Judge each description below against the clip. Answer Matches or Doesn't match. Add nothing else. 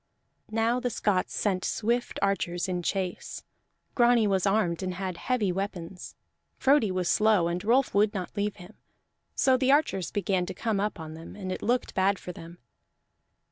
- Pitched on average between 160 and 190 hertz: Doesn't match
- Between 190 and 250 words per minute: Doesn't match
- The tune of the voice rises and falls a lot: Doesn't match